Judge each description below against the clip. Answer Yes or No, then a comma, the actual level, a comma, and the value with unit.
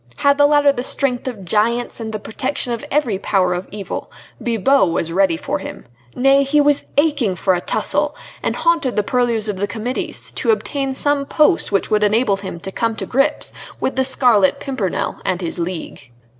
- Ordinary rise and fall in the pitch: No, wide, 6.0 semitones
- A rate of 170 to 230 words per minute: Yes, average, 195 wpm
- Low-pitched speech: No, high, 240 Hz